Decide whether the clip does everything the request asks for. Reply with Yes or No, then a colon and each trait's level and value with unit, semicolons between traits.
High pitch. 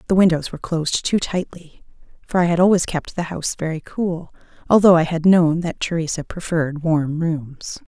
No: medium, 165 Hz